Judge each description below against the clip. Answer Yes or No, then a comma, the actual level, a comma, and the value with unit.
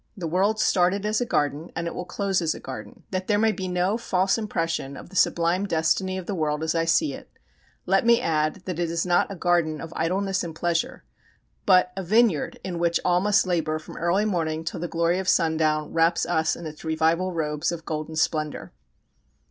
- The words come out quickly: Yes, fast, 210 wpm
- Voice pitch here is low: No, medium, 170 Hz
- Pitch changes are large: No, average, 2.9 semitones